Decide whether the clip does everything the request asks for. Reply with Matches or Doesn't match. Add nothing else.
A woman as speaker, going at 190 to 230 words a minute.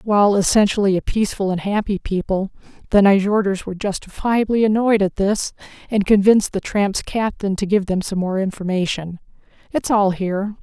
Doesn't match